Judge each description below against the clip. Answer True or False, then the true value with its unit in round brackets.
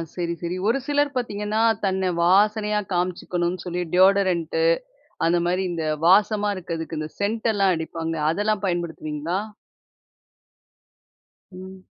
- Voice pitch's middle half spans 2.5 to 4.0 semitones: True (3.3 semitones)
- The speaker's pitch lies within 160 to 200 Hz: True (185 Hz)